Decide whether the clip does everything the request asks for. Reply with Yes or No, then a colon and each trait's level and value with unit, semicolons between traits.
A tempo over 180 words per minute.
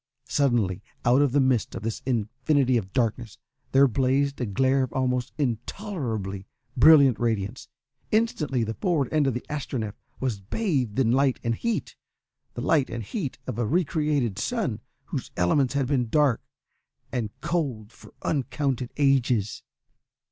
No: average, 150 wpm